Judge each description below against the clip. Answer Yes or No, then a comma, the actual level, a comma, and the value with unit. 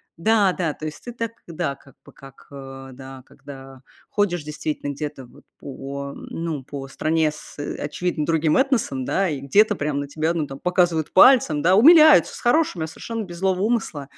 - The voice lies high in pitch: No, medium, 155 Hz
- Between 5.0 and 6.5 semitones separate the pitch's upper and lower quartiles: Yes, average, 5.3 semitones